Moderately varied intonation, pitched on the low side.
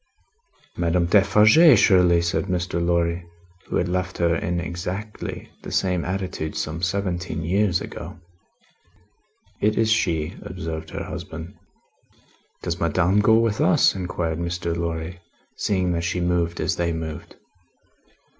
No: narrow, 1.8 semitones; very low, 85 Hz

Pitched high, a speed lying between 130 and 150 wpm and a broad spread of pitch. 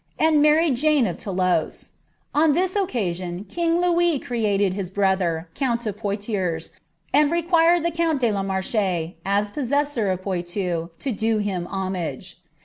Yes: high, 210 Hz; average, 140 wpm; wide, 8.2 semitones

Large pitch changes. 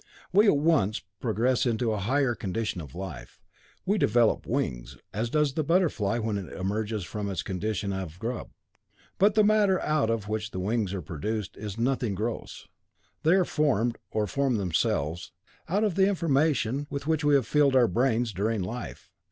Yes: wide, 6.1 semitones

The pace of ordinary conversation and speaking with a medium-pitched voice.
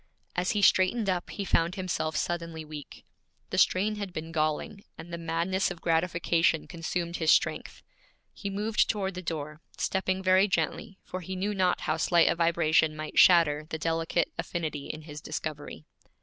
Yes: average, 170 wpm; medium, 170 Hz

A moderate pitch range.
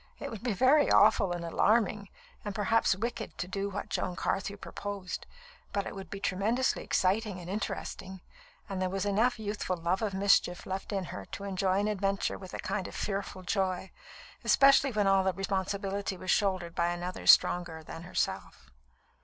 No: narrow, 1.9 semitones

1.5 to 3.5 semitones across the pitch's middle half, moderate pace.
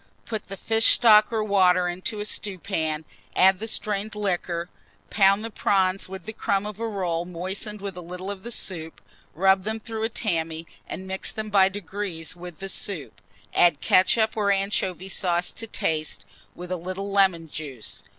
Yes: average, 3.0 semitones; average, 180 wpm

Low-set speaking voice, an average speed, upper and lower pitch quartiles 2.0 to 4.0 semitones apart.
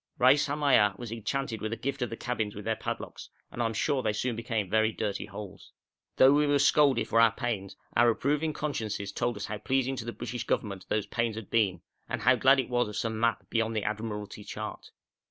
No: low, 115 Hz; fast, 225 wpm; average, 3.4 semitones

